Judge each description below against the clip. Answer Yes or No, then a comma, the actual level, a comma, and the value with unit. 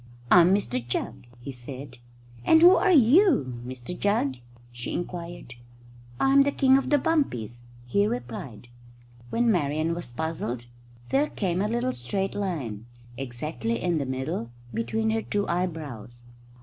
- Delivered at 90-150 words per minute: Yes, average, 140 wpm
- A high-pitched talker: No, medium, 160 Hz